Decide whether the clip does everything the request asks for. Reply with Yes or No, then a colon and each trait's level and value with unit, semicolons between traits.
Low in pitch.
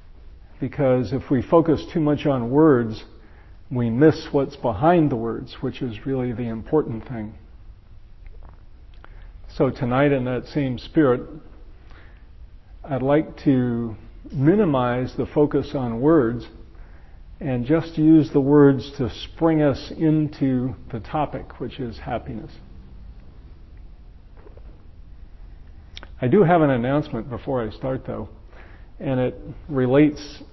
Yes: low, 120 Hz